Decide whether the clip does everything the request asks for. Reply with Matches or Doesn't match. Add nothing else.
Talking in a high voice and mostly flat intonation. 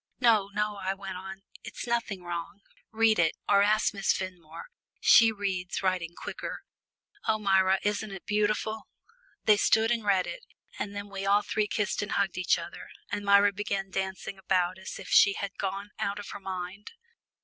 Matches